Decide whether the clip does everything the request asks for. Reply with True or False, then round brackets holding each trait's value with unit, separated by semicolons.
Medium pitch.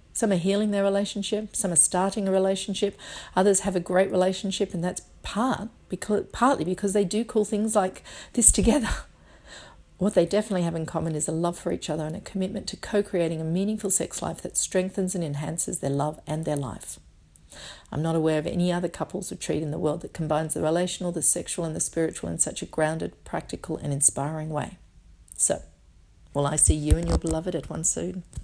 True (175 Hz)